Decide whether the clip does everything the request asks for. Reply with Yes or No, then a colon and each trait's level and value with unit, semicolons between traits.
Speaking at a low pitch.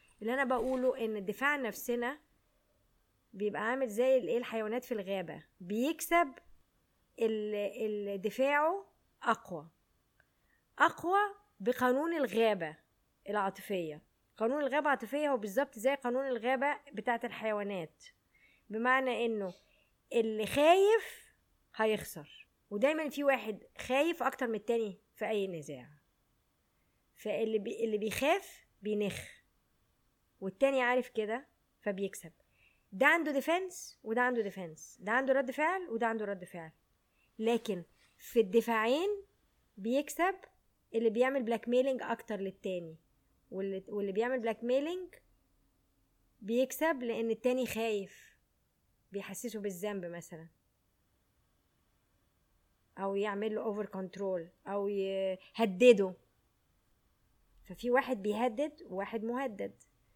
No: high, 225 Hz